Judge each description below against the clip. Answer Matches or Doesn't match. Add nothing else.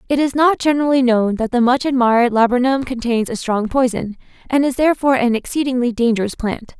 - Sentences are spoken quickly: Doesn't match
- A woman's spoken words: Matches